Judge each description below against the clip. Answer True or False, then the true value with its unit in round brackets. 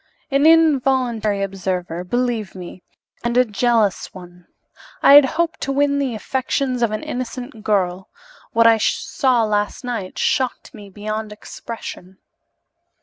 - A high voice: True (225 Hz)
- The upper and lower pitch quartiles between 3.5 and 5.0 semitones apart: True (4.4 semitones)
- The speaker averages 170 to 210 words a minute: False (135 wpm)